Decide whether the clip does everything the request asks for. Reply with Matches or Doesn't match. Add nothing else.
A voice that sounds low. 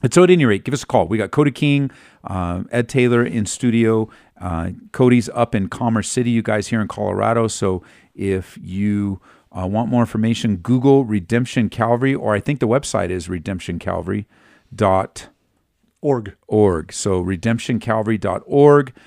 Matches